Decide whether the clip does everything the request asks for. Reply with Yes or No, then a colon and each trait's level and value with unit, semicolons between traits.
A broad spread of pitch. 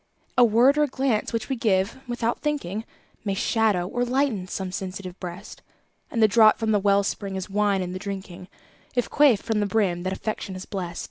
No: average, 3.6 semitones